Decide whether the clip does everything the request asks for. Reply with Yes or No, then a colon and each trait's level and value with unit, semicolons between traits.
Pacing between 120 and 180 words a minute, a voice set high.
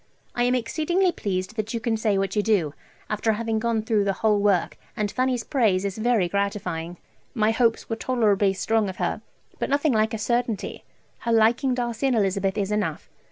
No: average, 195 wpm; high, 220 Hz